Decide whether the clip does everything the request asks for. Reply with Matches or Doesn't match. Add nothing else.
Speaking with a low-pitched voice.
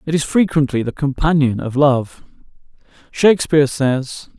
Doesn't match